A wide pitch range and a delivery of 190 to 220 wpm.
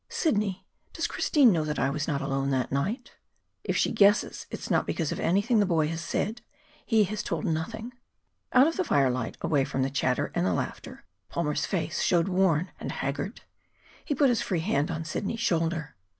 Yes: wide, 6.6 semitones; average, 195 wpm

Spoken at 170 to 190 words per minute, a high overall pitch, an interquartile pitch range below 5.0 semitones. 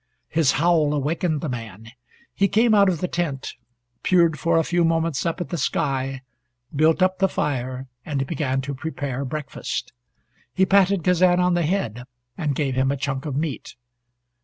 No: average, 175 wpm; medium, 155 Hz; average, 4.5 semitones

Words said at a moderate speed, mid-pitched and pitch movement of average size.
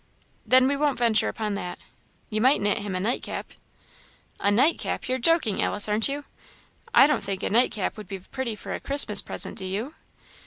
No: average, 190 wpm; high, 220 Hz; average, 4.6 semitones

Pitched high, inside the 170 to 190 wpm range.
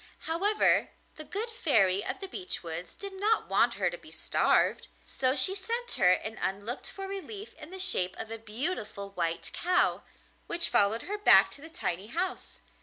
Yes: very high, 320 Hz; average, 180 wpm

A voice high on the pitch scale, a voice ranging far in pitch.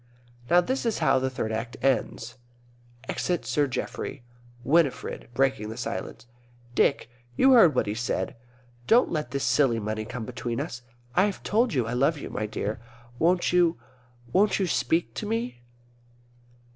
No: low, 135 Hz; wide, 6.8 semitones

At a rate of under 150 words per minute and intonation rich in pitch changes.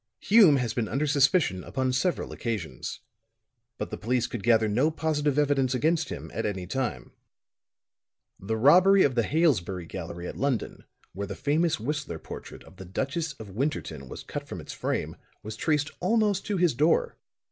No: average, 170 wpm; wide, 6.6 semitones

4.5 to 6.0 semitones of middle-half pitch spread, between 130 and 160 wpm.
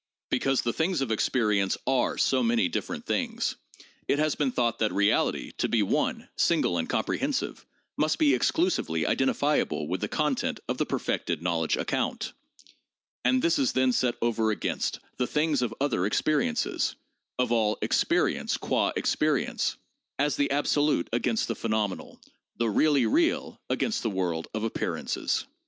Yes: average, 5.2 semitones; average, 155 wpm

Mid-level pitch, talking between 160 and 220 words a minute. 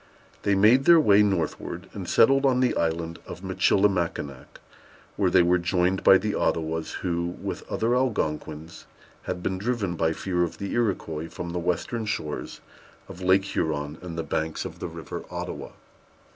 No: very low, 90 Hz; average, 165 wpm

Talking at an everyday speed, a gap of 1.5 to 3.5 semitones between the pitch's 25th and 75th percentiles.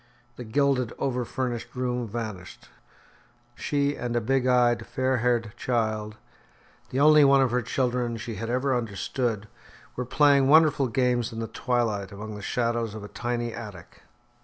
Yes: average, 160 wpm; narrow, 2.6 semitones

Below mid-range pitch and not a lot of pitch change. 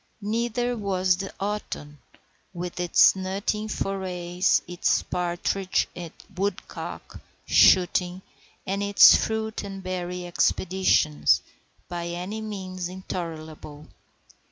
No: medium, 185 Hz; narrow, 2.1 semitones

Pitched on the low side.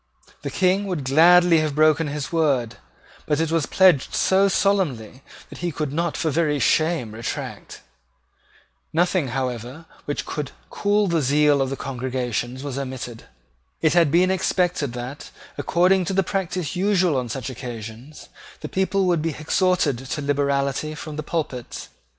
No: medium, 150 Hz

